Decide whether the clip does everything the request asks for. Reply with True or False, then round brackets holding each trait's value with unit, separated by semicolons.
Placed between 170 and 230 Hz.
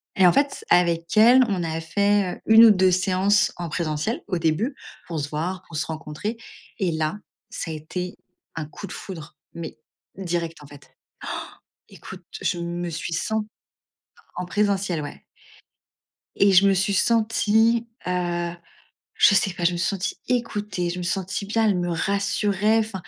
True (185 Hz)